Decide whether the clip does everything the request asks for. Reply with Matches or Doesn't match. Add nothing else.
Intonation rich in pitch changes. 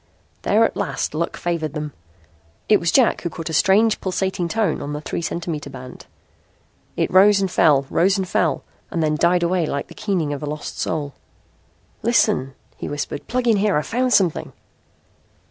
Doesn't match